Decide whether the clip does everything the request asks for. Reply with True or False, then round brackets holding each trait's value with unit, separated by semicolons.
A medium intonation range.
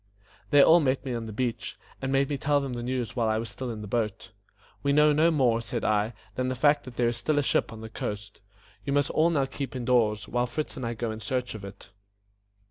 True (3.8 semitones)